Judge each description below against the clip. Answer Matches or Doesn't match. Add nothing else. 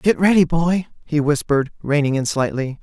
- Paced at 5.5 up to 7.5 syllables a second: Doesn't match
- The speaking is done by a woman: Doesn't match